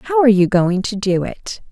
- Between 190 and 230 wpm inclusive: No, fast, 245 wpm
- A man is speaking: No, female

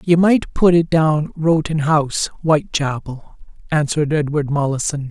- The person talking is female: No, male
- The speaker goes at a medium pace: No, slow, 130 wpm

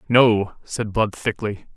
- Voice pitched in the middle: No, low, 110 Hz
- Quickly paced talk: No, slow, 135 wpm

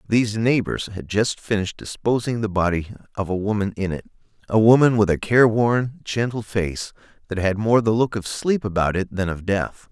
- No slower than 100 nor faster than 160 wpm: No, average, 190 wpm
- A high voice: No, low, 105 Hz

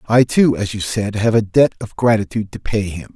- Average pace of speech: No, fast, 245 wpm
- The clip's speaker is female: No, male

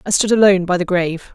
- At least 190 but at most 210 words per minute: No, fast, 265 wpm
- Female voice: Yes, female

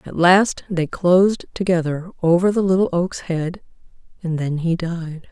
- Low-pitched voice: No, medium, 175 Hz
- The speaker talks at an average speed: Yes, average, 160 wpm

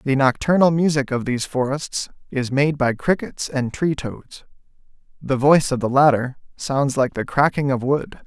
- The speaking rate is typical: Yes, average, 175 wpm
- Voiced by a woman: No, male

